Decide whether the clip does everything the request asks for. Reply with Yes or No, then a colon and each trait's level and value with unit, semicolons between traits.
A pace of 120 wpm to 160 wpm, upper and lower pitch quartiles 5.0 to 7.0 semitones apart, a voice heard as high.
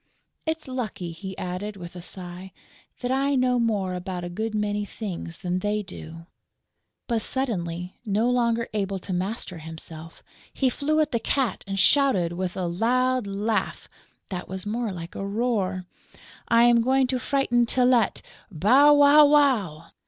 Yes: average, 155 wpm; wide, 5.5 semitones; high, 210 Hz